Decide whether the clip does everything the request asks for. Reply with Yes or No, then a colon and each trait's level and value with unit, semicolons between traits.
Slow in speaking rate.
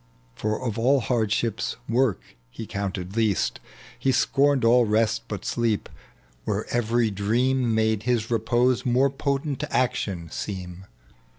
Yes: slow, 125 wpm